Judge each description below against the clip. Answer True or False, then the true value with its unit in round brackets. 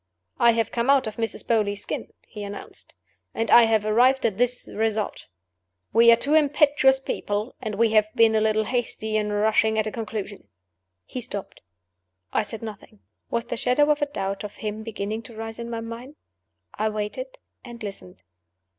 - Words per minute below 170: False (180 wpm)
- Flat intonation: True (2.1 semitones)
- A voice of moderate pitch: False (225 Hz)